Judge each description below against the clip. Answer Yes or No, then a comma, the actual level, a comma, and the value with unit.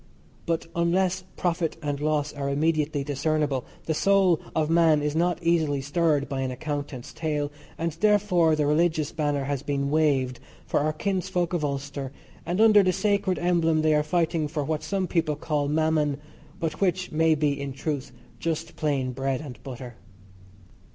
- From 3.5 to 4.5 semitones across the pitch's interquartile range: No, average, 2.8 semitones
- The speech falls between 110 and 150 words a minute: No, average, 165 wpm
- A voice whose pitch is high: No, medium, 155 Hz